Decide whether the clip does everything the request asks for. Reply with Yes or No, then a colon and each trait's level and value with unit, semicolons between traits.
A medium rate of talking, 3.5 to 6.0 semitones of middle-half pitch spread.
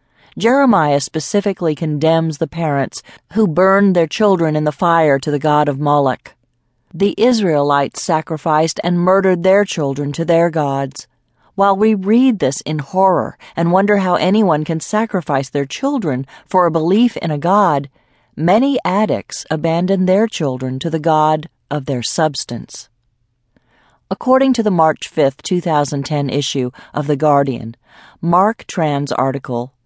Yes: average, 145 wpm; average, 5.1 semitones